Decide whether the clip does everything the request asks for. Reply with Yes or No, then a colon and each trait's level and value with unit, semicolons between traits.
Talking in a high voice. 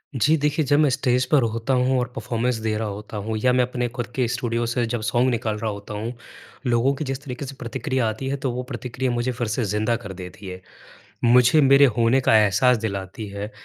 No: low, 120 Hz